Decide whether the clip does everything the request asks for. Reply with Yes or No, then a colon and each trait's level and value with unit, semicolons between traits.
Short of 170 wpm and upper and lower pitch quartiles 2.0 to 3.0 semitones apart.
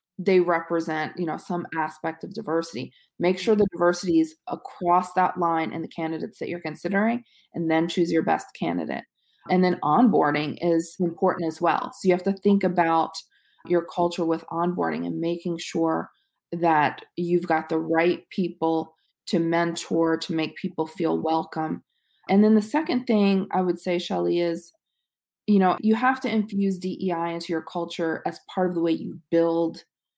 No: average, 175 wpm; narrow, 2.5 semitones